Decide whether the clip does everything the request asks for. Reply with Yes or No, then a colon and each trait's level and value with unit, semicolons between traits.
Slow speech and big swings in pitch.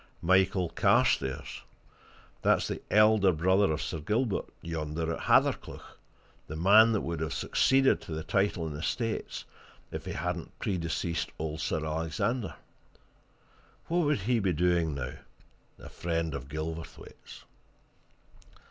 No: slow, 130 wpm; average, 4.4 semitones